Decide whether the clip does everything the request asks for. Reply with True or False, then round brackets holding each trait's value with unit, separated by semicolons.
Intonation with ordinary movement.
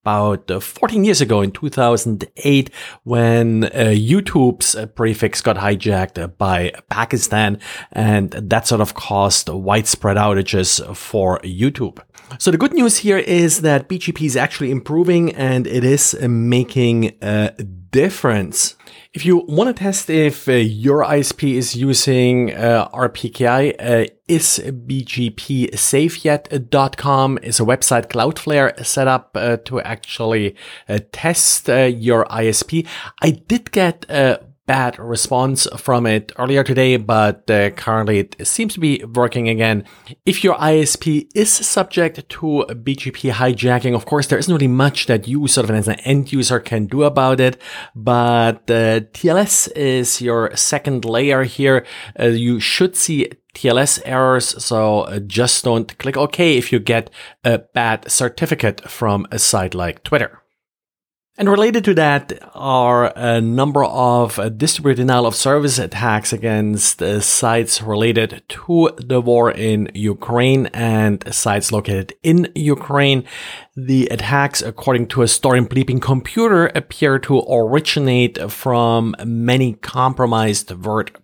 True (4.0 semitones)